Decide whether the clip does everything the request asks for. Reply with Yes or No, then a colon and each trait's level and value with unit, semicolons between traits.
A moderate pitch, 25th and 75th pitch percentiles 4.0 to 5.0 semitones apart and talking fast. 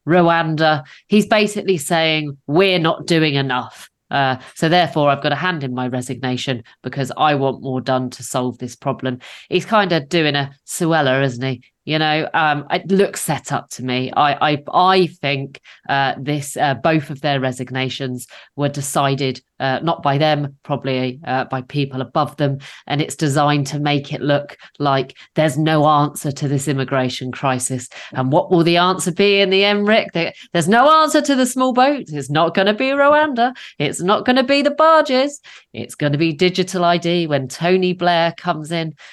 No: medium, 150 Hz; average, 4.7 semitones; average, 190 wpm